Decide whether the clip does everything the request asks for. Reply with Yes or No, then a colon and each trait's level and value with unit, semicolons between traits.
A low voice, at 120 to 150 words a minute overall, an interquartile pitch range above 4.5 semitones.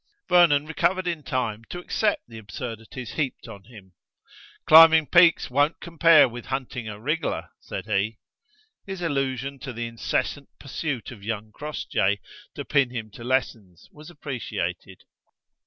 Yes: low, 130 Hz; average, 140 wpm; wide, 5.5 semitones